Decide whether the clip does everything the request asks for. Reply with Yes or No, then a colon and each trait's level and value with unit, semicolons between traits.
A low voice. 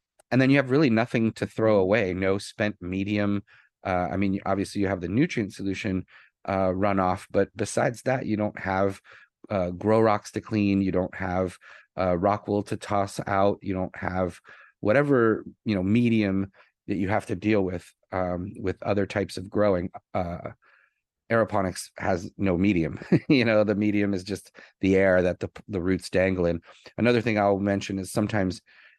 Yes: low, 100 Hz